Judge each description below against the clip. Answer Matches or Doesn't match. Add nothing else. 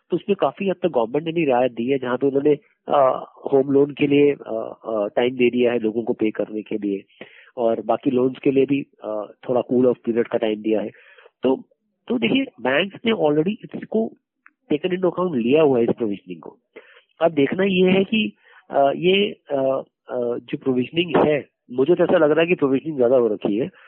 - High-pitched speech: Doesn't match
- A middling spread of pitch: Doesn't match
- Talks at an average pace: Doesn't match